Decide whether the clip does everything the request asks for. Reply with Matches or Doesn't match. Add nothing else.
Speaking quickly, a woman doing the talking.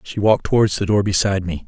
Doesn't match